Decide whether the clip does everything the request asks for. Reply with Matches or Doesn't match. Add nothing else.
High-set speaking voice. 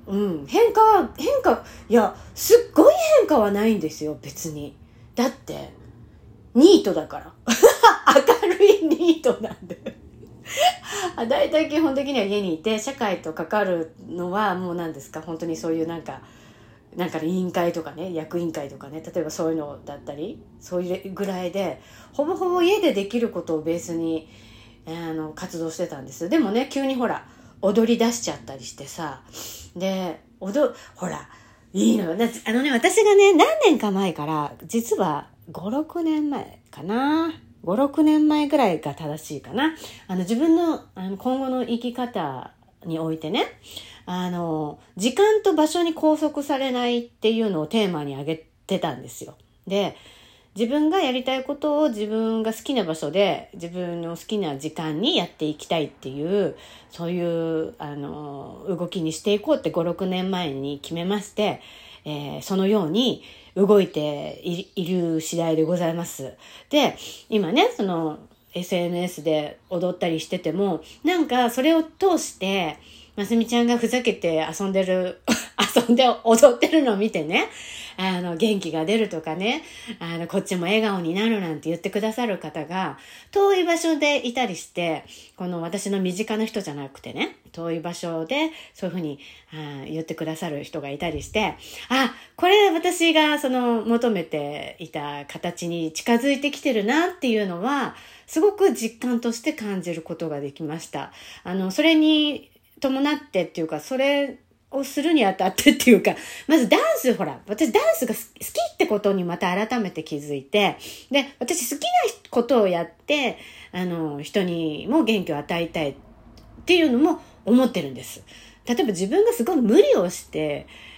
Matches